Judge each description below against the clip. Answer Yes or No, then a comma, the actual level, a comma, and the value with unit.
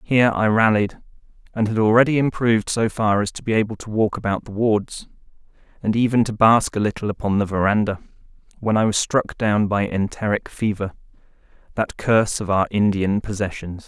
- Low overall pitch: Yes, low, 105 Hz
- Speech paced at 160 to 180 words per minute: Yes, average, 175 wpm